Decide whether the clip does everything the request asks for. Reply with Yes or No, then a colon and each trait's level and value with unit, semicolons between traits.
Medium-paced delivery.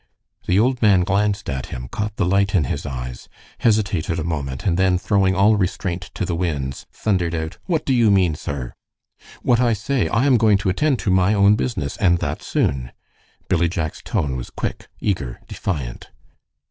Yes: average, 185 wpm